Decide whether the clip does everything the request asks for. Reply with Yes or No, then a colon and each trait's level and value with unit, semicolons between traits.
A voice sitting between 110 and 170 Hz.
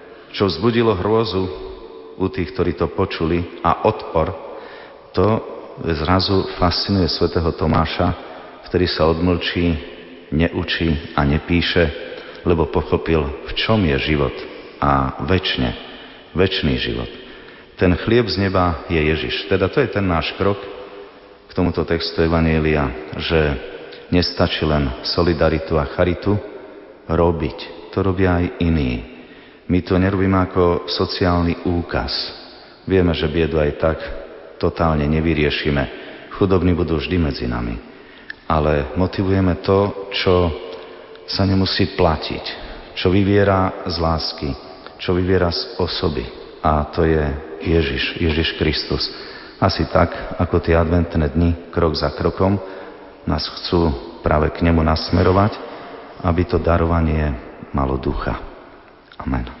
No: very low, 85 Hz